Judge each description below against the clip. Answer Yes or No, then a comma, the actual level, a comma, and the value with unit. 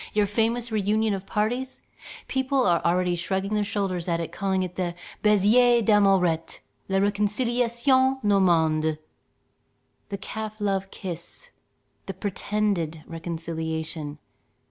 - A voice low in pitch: No, high, 200 Hz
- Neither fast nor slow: No, slow, 115 wpm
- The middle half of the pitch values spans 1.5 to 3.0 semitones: No, average, 3.9 semitones